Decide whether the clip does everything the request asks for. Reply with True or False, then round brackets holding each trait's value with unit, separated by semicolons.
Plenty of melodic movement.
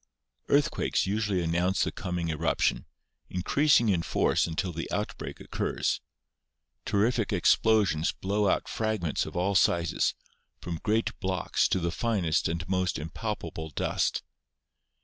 False (4.0 semitones)